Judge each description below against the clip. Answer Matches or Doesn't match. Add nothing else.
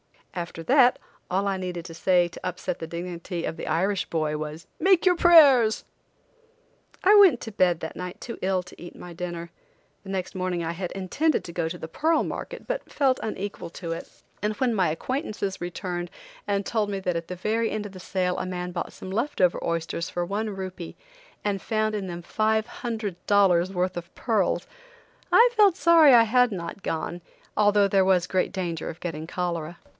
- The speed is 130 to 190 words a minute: Doesn't match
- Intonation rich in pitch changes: Doesn't match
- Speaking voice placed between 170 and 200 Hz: Matches